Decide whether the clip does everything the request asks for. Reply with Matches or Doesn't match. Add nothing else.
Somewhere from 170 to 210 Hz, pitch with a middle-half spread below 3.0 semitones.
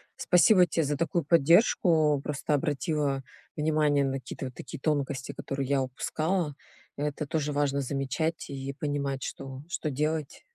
Doesn't match